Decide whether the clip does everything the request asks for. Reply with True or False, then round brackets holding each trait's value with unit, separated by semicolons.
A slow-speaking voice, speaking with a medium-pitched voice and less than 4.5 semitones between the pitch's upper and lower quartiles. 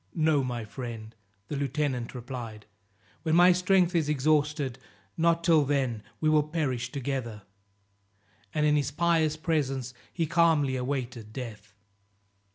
True (130 wpm; 145 Hz; 4.1 semitones)